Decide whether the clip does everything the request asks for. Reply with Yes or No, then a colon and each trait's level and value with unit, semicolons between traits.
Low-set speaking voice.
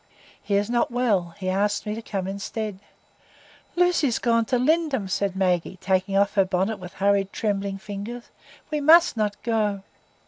No: high, 205 Hz